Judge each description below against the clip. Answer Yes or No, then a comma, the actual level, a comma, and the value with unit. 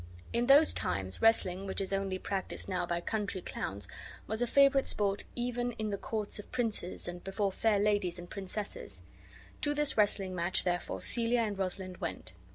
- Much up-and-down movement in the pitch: No, average, 3.6 semitones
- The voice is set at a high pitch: Yes, high, 200 Hz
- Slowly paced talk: No, average, 175 wpm